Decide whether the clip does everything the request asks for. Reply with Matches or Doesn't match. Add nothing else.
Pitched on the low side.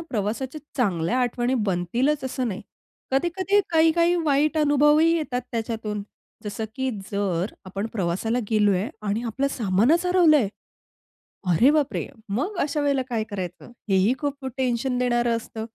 Doesn't match